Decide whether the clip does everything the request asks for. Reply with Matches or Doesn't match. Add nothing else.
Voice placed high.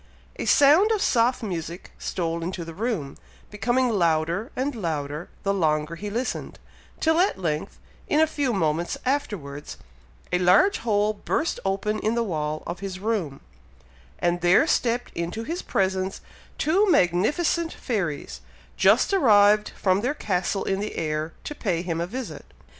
Matches